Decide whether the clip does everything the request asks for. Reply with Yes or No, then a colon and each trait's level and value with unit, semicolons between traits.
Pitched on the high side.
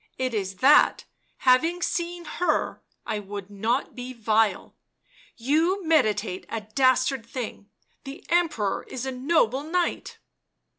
Yes: very high, 255 Hz